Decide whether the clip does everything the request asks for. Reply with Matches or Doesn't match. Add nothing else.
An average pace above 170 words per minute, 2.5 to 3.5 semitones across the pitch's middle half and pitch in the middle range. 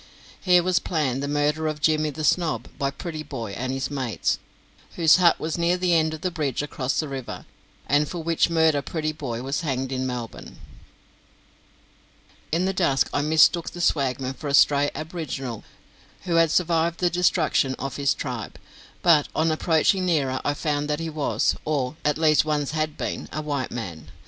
Matches